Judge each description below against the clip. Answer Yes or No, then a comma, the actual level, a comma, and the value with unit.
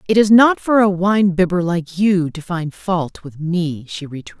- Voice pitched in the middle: Yes, medium, 180 Hz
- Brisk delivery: Yes, fast, 220 wpm